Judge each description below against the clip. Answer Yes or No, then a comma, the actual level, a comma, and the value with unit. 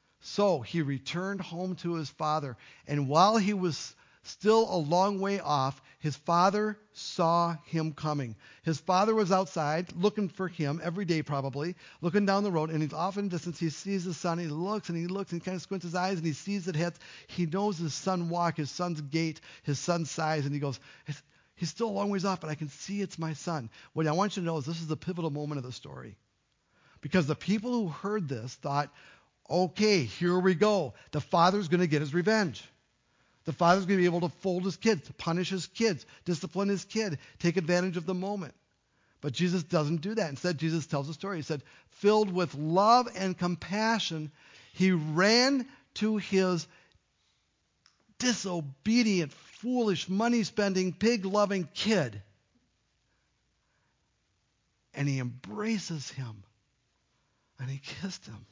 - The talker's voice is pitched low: No, medium, 175 Hz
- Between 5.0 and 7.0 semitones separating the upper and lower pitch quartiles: No, average, 4.4 semitones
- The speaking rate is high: No, average, 180 wpm